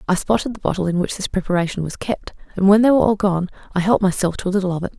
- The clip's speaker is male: No, female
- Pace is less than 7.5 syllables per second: No, 7.6 syllables/s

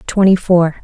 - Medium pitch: Yes, medium, 180 Hz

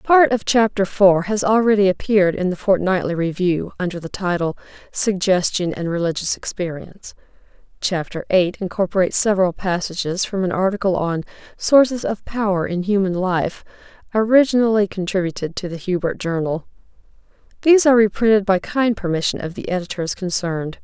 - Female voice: Yes, female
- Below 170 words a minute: Yes, average, 140 wpm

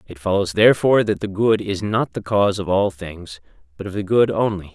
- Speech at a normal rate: No, fast, 225 wpm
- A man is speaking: Yes, male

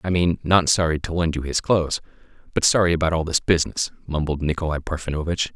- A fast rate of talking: No, average, 195 wpm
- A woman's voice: No, male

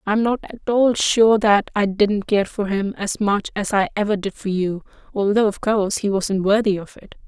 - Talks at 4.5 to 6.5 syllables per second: Yes, 5.0 syllables/s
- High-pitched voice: Yes, high, 205 Hz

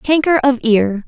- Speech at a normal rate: Yes, average, 165 wpm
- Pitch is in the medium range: No, very high, 255 Hz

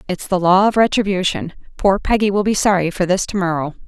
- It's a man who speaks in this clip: No, female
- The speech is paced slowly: No, average, 200 wpm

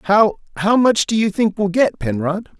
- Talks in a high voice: Yes, high, 200 Hz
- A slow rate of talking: No, average, 185 wpm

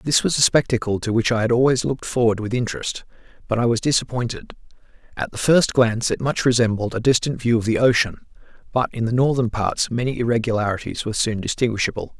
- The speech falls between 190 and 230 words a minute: Yes, average, 195 wpm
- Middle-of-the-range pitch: No, low, 120 Hz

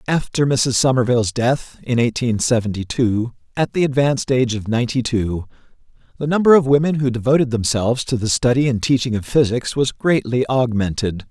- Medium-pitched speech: No, low, 125 Hz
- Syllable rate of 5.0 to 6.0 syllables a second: Yes, 5.5 syllables/s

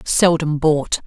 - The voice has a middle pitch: Yes, medium, 155 Hz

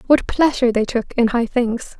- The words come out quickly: Yes, fast, 210 wpm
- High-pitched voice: Yes, high, 240 Hz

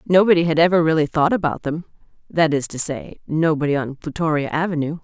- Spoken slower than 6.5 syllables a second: Yes, 5.9 syllables/s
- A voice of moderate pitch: Yes, medium, 160 Hz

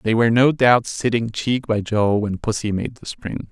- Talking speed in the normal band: No, fast, 220 wpm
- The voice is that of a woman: No, male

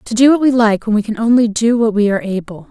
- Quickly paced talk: Yes, fast, 310 wpm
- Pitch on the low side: No, high, 220 Hz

